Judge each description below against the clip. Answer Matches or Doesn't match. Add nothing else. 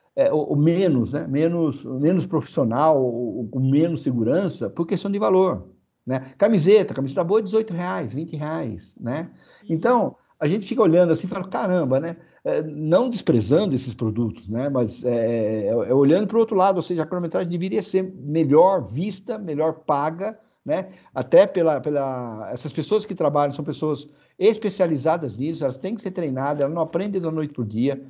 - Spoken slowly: Doesn't match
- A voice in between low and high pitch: Matches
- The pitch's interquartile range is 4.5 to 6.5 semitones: Matches